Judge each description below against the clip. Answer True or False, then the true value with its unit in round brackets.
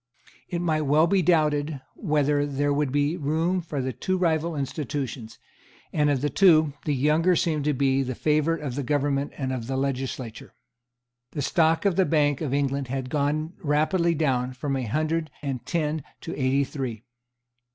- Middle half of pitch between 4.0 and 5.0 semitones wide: False (2.7 semitones)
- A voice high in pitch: False (145 Hz)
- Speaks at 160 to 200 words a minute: True (175 wpm)